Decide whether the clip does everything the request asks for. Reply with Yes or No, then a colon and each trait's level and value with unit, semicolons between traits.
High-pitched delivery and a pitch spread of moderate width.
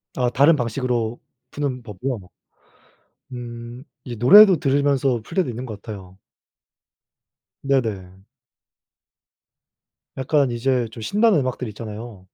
No: low, 125 Hz; average, 3.5 semitones